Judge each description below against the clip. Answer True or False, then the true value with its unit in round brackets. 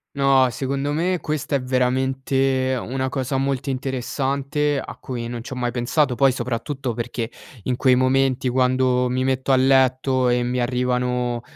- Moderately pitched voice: False (130 Hz)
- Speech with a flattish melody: True (1.3 semitones)